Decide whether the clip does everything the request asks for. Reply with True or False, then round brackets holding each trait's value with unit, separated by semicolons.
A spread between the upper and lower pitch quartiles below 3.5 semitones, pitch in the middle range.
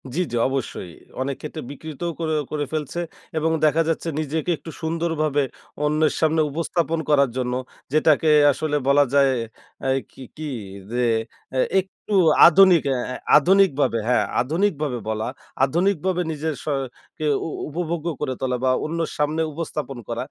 True (2.9 semitones; 155 Hz)